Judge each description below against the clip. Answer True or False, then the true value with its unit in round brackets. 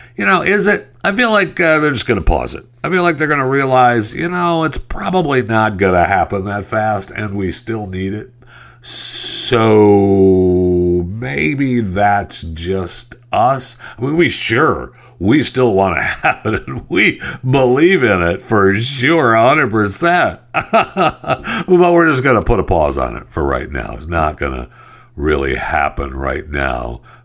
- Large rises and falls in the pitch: True (7.3 semitones)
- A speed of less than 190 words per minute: True (175 wpm)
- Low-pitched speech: True (110 Hz)